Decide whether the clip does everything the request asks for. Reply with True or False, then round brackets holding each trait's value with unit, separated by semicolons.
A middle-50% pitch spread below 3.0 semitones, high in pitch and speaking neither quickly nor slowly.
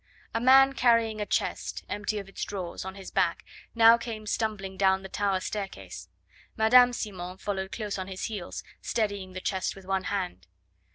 True (2.6 semitones; 200 Hz; 175 wpm)